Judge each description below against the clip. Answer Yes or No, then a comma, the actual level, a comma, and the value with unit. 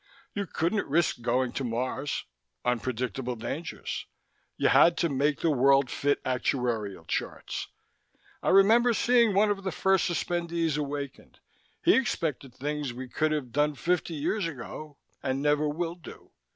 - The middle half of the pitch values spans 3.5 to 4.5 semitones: No, average, 4.9 semitones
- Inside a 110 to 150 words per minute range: Yes, average, 145 wpm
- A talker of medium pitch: Yes, medium, 150 Hz